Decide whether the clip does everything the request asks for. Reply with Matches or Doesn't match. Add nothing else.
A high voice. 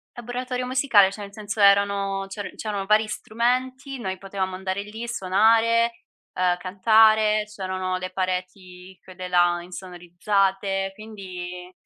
Matches